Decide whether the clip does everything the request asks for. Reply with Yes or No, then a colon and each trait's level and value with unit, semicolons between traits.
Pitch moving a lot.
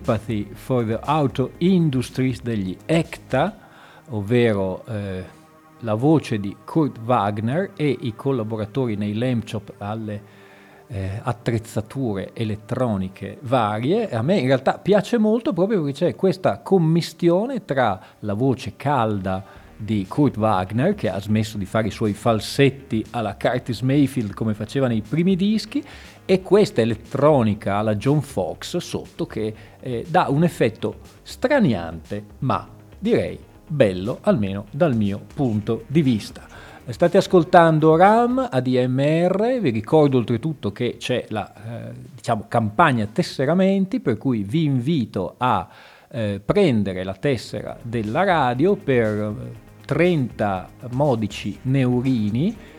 Yes: wide, 6.2 semitones